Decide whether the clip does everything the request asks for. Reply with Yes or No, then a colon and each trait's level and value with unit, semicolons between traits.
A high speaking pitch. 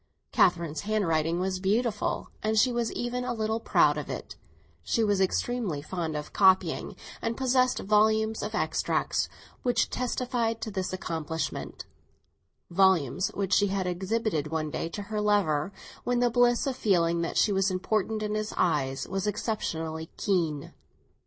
Yes: high, 195 Hz